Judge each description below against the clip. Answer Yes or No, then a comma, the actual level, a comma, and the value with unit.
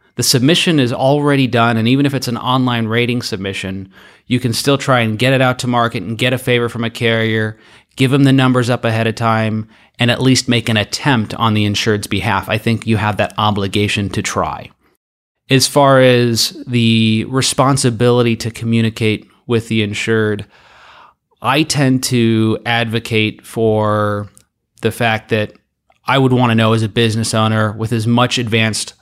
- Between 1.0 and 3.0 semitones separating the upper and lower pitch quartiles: Yes, narrow, 2.4 semitones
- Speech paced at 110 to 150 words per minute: No, average, 180 wpm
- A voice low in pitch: Yes, low, 115 Hz